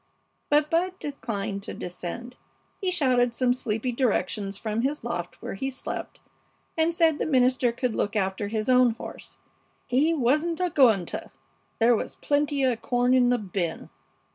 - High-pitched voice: Yes, high, 245 Hz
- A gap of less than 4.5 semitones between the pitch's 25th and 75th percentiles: No, average, 4.9 semitones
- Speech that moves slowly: No, average, 150 wpm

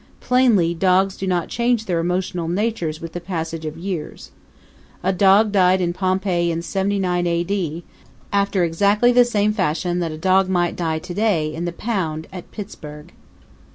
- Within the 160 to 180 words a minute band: Yes, average, 170 wpm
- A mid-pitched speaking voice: Yes, medium, 180 Hz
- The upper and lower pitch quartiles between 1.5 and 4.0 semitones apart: Yes, average, 3.0 semitones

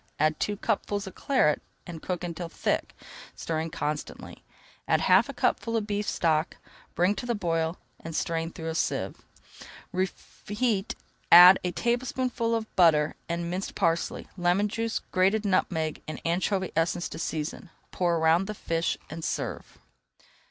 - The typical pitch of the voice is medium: Yes, medium, 175 Hz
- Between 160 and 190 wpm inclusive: No, average, 150 wpm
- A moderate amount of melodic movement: Yes, average, 3.9 semitones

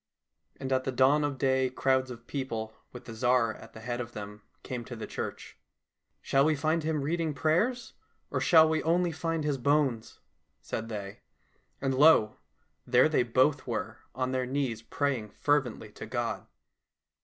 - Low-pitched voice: Yes, low, 130 Hz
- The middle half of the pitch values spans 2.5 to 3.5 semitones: No, average, 3.9 semitones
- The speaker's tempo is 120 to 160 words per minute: No, average, 175 wpm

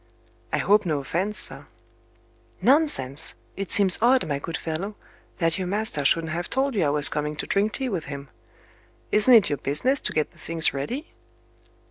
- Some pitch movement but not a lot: No, wide, 6.2 semitones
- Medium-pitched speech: Yes, medium, 175 Hz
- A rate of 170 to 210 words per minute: Yes, average, 180 wpm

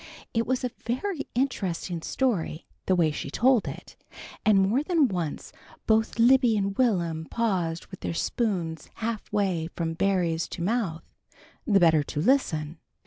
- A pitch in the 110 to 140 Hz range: No, high, 195 Hz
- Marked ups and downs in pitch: Yes, wide, 6.1 semitones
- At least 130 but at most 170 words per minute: Yes, average, 150 wpm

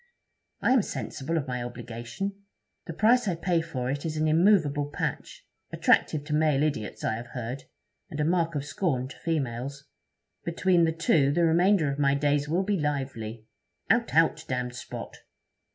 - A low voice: No, medium, 150 Hz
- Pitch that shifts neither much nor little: Yes, average, 4.2 semitones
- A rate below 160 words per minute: No, average, 170 wpm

